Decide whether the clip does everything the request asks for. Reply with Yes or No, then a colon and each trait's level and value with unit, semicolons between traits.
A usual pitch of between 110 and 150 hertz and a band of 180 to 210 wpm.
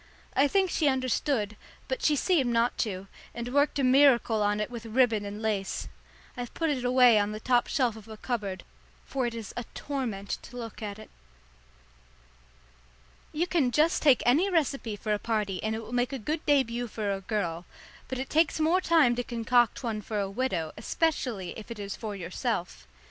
No: high, 235 Hz; average, 195 wpm